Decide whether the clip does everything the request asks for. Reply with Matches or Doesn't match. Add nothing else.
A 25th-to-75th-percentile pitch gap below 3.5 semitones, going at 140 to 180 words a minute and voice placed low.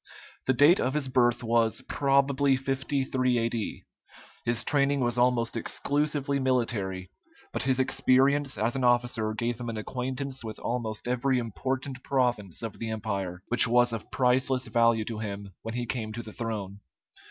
Matches